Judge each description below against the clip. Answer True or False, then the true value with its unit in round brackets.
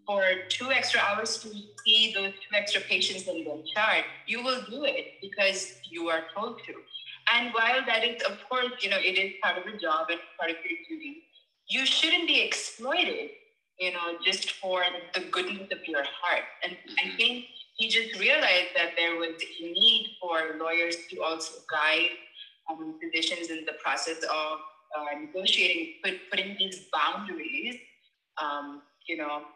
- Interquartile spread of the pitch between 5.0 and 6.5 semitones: True (5.4 semitones)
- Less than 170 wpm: False (175 wpm)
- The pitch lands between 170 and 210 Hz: True (190 Hz)